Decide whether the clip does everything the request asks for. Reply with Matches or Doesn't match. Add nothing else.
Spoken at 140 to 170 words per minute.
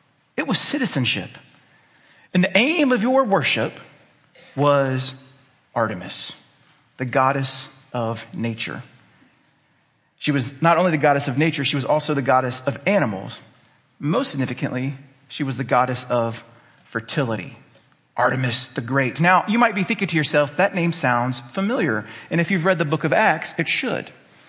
Matches